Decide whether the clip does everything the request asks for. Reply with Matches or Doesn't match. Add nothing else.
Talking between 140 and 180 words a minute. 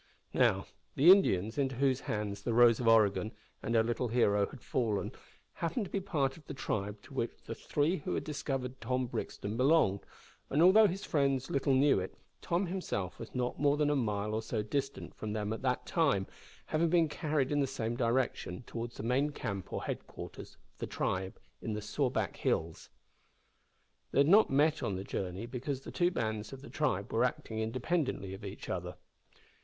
Doesn't match